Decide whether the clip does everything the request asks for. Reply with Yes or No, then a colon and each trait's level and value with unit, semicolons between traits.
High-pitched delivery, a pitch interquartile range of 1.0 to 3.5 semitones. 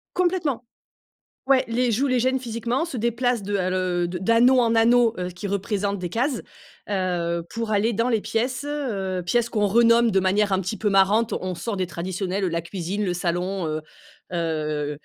No: high, 205 Hz; average, 4.4 semitones